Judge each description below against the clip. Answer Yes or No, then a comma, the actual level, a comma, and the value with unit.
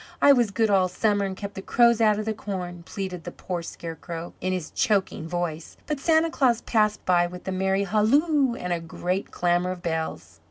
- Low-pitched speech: No, high, 190 Hz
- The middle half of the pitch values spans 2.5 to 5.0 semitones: Yes, average, 3.9 semitones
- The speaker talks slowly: No, fast, 205 wpm